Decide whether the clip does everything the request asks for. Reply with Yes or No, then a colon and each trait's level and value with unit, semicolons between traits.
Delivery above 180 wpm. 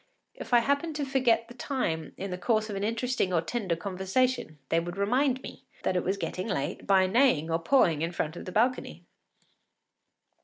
Yes: average, 190 wpm